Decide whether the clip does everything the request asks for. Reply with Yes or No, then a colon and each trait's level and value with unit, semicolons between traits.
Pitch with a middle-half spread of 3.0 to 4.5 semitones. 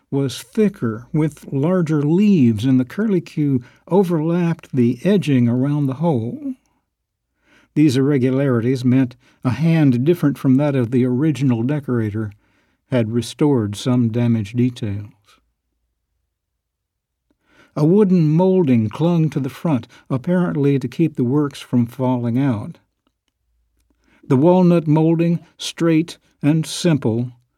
No: average, 5.1 semitones